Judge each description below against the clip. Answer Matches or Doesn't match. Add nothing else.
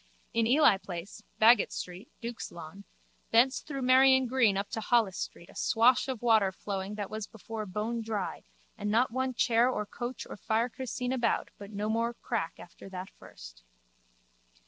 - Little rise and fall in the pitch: Doesn't match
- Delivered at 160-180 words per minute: Matches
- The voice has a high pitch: Matches